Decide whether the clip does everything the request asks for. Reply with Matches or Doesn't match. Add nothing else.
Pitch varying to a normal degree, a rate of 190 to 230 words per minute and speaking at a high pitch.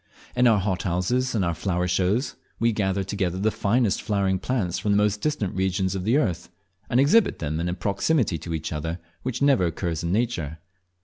Doesn't match